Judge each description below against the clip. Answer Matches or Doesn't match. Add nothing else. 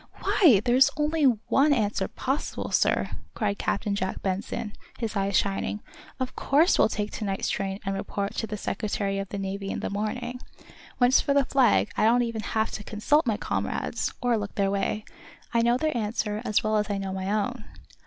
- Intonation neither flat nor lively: Matches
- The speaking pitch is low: Doesn't match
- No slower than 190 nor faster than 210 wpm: Matches